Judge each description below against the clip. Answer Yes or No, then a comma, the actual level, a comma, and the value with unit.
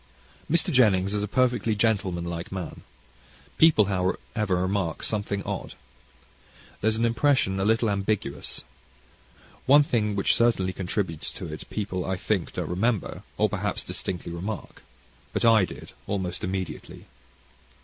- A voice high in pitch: No, low, 100 Hz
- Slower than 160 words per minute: Yes, slow, 135 wpm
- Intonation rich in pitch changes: No, average, 3.4 semitones